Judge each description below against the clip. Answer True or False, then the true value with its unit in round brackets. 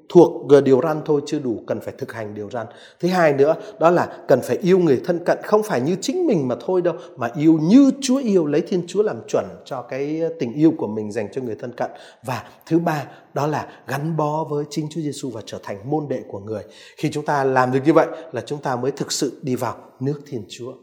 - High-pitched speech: False (155 Hz)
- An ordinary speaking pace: False (255 wpm)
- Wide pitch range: False (4.3 semitones)